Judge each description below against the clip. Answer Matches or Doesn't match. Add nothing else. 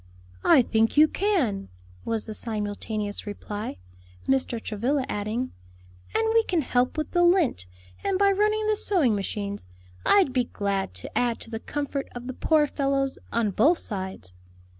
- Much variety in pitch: Matches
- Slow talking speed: Doesn't match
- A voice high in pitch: Matches